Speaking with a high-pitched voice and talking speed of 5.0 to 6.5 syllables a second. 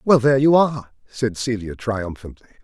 No: low, 125 Hz; 5.4 syllables/s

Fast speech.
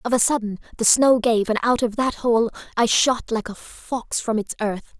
Yes: fast, 230 wpm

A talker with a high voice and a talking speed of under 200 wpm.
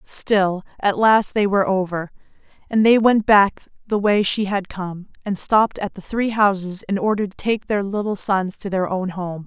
No: high, 200 Hz; fast, 205 wpm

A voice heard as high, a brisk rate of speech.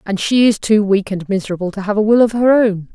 Yes: high, 210 Hz; fast, 285 wpm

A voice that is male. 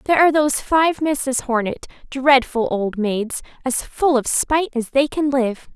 No: female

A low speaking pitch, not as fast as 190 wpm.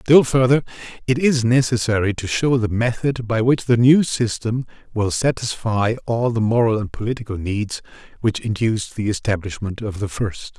Yes: low, 115 Hz; average, 165 wpm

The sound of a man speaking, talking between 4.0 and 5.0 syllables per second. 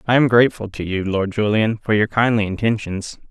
No: male; 5.7 syllables/s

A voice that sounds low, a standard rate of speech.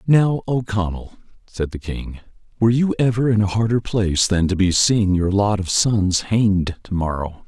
Yes: low, 100 Hz; average, 195 wpm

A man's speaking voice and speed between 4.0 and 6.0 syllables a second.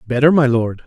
Yes: male; 5.6 syllables/s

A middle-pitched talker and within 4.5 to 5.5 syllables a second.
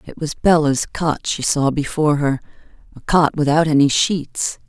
Yes: medium, 150 Hz; 4.6 syllables/s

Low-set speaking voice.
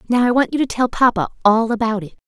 No: high, 230 Hz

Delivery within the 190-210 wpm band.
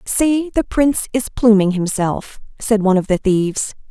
No: average, 170 wpm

